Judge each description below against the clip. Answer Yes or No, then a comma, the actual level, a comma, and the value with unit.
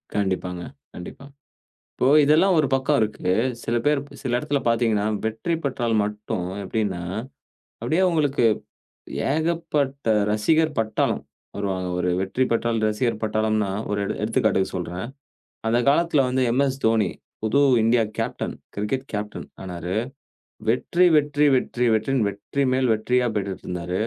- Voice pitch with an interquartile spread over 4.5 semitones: Yes, average, 5.0 semitones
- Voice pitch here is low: Yes, low, 115 Hz